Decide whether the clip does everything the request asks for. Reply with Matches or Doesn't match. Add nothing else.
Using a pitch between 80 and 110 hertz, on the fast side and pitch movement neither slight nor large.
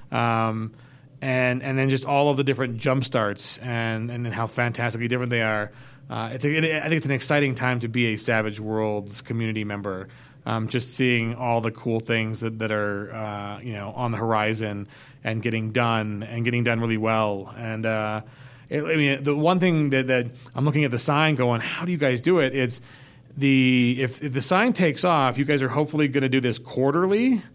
Doesn't match